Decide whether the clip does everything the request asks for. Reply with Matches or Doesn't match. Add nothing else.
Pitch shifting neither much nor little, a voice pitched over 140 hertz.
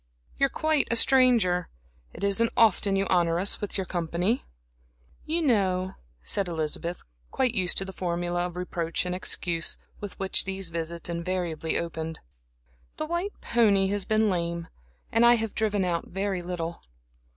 Matches